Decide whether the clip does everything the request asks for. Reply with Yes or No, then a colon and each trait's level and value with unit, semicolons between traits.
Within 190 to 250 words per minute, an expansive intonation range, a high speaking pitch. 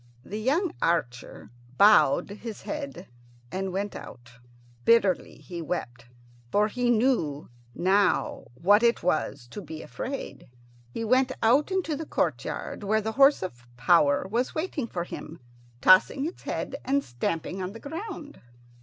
No: average, 145 wpm; wide, 7.5 semitones; high, 205 Hz